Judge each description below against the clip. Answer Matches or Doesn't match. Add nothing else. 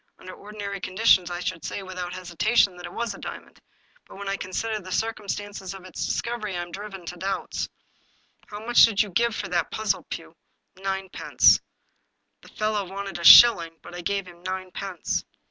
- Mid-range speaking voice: Doesn't match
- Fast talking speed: Doesn't match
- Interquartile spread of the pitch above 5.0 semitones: Doesn't match